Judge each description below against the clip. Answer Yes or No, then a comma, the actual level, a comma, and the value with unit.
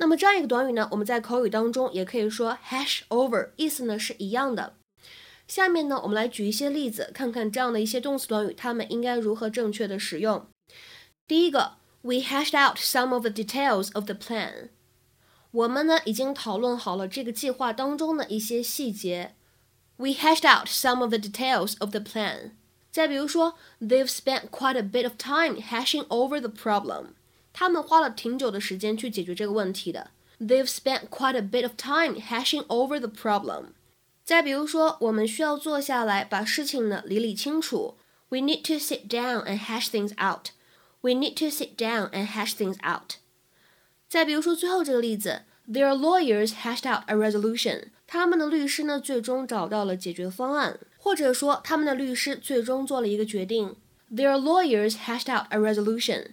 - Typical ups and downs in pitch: Yes, average, 4.3 semitones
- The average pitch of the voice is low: No, high, 245 Hz